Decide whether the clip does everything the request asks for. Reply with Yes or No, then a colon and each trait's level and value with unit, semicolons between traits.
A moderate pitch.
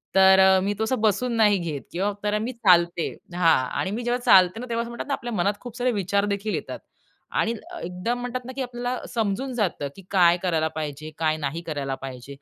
No: high, 200 Hz